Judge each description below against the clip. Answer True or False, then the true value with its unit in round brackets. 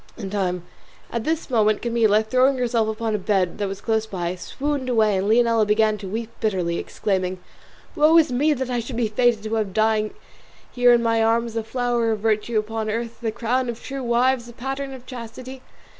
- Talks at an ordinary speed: True (195 wpm)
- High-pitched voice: True (230 Hz)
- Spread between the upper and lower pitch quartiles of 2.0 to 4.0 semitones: True (2.4 semitones)